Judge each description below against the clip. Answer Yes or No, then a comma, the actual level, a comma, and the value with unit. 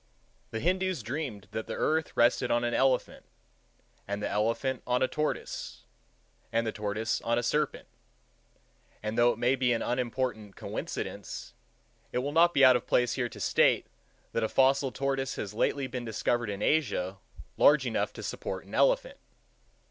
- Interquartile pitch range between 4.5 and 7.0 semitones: No, average, 3.4 semitones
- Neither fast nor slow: Yes, average, 170 wpm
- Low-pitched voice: Yes, low, 125 Hz